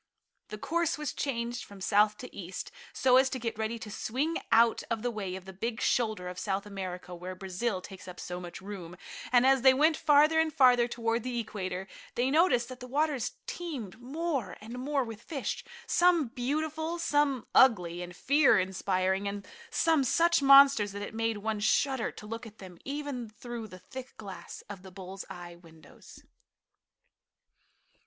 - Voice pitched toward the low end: No, high, 230 Hz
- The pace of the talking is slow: No, average, 180 wpm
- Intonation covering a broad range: Yes, wide, 5.7 semitones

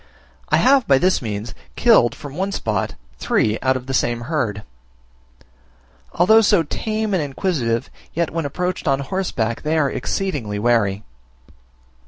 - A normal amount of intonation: No, wide, 7.7 semitones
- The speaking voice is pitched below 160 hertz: Yes, medium, 140 Hz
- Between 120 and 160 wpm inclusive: Yes, average, 145 wpm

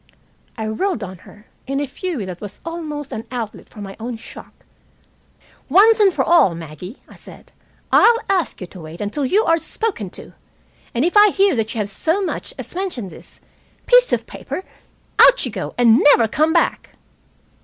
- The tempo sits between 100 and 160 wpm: No, average, 185 wpm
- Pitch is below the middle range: No, very high, 260 Hz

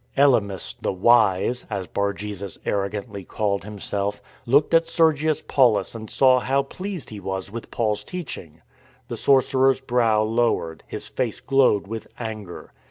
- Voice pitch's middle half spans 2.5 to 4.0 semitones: No, average, 4.7 semitones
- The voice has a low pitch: Yes, low, 110 Hz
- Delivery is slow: No, average, 155 wpm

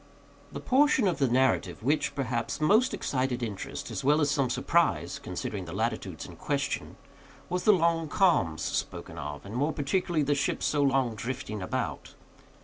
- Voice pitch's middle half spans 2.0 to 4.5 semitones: No, average, 5.0 semitones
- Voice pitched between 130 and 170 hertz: Yes, medium, 140 Hz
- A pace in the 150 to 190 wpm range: Yes, average, 165 wpm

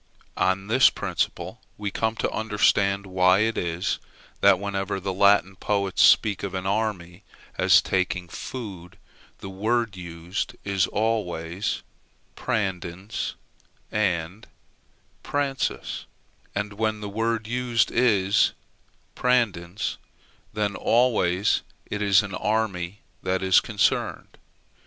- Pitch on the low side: Yes, low, 100 Hz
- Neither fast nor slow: No, slow, 110 wpm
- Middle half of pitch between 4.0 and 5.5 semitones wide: No, average, 2.8 semitones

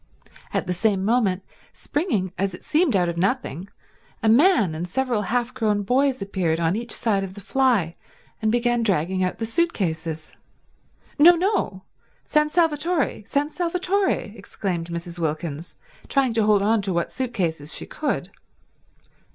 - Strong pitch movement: Yes, wide, 6.6 semitones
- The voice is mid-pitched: No, high, 210 Hz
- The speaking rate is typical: Yes, average, 150 wpm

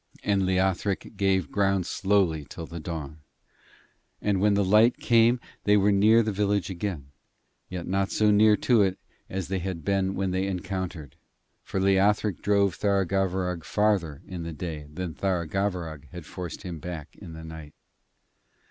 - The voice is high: No, very low, 95 Hz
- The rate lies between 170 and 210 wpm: No, average, 155 wpm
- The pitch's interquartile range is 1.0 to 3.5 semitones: Yes, average, 3.0 semitones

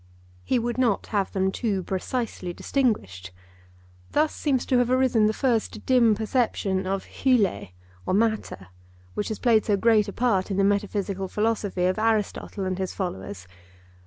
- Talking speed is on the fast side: No, average, 160 wpm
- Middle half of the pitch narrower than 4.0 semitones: Yes, average, 3.6 semitones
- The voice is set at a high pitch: Yes, high, 210 Hz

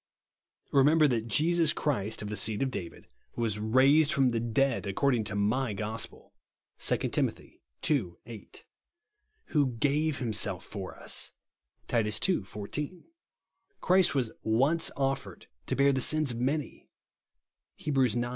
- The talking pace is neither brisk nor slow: Yes, average, 145 wpm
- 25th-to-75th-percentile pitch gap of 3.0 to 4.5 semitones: No, average, 5.2 semitones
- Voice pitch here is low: Yes, low, 125 Hz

